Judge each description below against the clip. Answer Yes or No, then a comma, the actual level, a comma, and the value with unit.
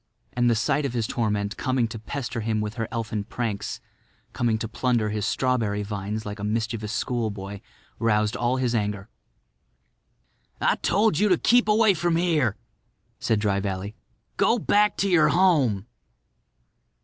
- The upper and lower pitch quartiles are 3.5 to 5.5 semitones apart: Yes, average, 4.0 semitones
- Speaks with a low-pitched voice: Yes, low, 115 Hz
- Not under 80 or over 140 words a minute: No, average, 150 wpm